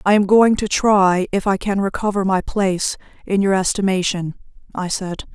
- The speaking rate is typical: Yes, average, 180 wpm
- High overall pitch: Yes, high, 195 Hz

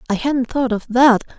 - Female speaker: Yes, female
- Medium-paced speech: No, fast, 215 wpm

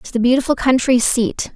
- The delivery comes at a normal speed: Yes, average, 195 wpm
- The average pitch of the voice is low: No, high, 245 Hz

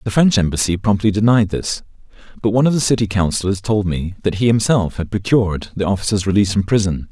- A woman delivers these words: No, male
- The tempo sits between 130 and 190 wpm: No, average, 200 wpm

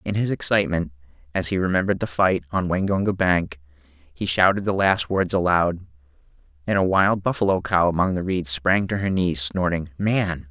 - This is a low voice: Yes, very low, 90 Hz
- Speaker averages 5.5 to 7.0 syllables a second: No, 5.2 syllables/s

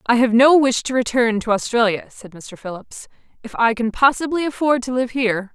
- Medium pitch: No, high, 240 Hz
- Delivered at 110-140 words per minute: No, fast, 205 wpm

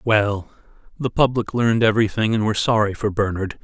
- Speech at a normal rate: Yes, average, 165 wpm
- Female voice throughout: No, male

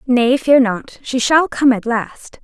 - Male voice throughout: No, female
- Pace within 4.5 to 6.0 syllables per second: No, 3.5 syllables/s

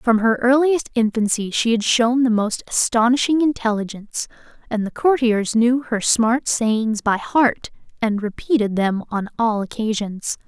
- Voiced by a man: No, female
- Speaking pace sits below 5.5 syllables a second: Yes, 4.4 syllables/s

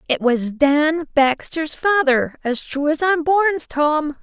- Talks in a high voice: Yes, very high, 300 Hz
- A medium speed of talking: Yes, average, 155 wpm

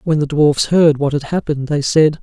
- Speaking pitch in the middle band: Yes, medium, 150 Hz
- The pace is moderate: No, fast, 240 wpm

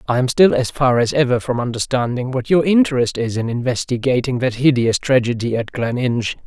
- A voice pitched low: Yes, low, 130 Hz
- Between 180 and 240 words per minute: Yes, average, 185 wpm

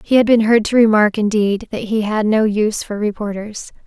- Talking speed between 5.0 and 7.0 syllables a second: Yes, 5.2 syllables/s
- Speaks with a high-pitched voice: Yes, high, 215 Hz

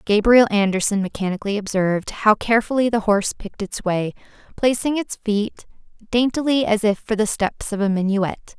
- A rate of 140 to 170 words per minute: Yes, average, 160 wpm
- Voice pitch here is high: Yes, high, 215 Hz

